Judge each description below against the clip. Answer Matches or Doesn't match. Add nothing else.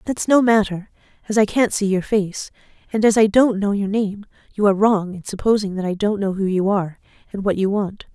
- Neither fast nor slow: Doesn't match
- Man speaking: Doesn't match